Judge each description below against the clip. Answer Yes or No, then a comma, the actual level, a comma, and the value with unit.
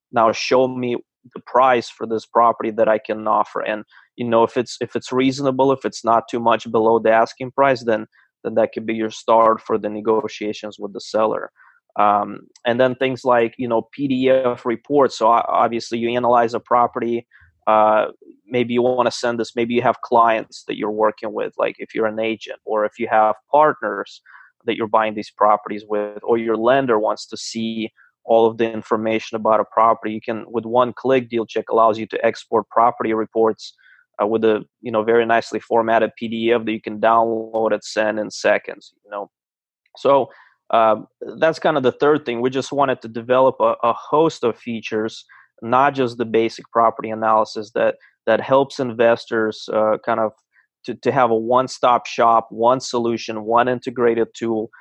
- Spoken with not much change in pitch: Yes, narrow, 1.8 semitones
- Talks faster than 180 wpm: Yes, average, 190 wpm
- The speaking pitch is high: No, low, 115 Hz